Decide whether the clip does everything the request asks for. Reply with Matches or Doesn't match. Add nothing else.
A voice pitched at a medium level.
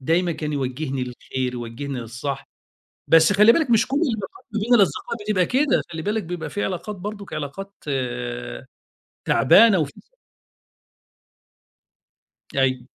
Matches